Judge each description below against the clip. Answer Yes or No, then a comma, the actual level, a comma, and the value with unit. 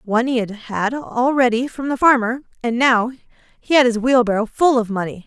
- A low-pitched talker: No, high, 240 Hz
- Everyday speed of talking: Yes, average, 195 wpm